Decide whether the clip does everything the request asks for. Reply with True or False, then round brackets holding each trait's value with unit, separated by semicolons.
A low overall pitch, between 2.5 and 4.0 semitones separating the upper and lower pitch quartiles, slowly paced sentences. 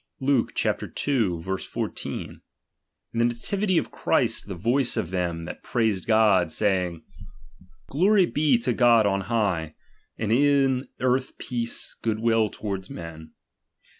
False (115 Hz; 5.3 semitones; 130 wpm)